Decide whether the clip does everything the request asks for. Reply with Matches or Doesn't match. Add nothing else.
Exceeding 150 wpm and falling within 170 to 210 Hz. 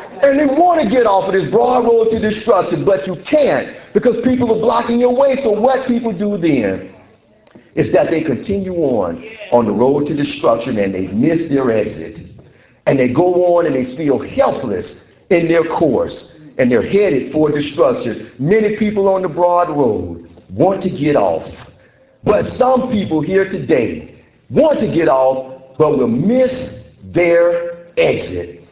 Matches